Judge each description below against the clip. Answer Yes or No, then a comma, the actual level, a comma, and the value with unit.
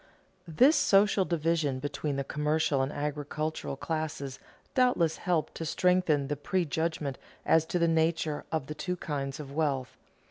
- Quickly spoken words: No, average, 145 wpm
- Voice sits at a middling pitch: Yes, medium, 155 Hz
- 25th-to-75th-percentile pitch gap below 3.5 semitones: Yes, average, 2.7 semitones